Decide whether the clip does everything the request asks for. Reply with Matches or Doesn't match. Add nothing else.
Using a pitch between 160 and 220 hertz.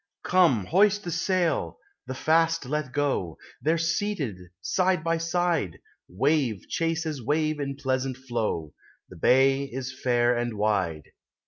Doesn't match